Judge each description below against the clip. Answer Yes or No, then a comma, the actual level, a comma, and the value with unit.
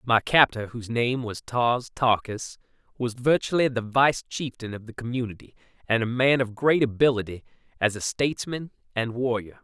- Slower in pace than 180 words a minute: Yes, average, 160 wpm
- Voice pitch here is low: Yes, low, 120 Hz